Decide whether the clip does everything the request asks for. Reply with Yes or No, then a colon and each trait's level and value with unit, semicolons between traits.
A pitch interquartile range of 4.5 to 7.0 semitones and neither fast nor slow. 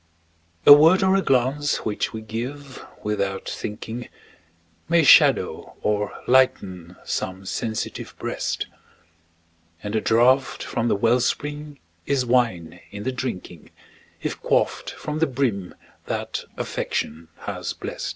No: average, 5.1 semitones; slow, 125 wpm